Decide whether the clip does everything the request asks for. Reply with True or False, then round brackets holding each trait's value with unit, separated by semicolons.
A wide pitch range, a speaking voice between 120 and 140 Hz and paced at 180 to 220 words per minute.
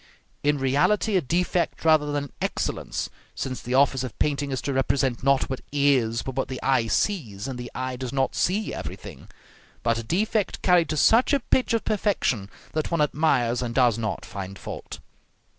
False (4.7 semitones; 135 Hz; 190 wpm)